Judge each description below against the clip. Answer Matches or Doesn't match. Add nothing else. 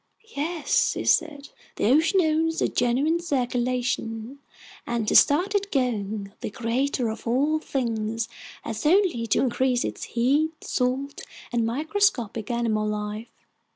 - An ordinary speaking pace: Doesn't match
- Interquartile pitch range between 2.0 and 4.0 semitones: Doesn't match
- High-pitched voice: Matches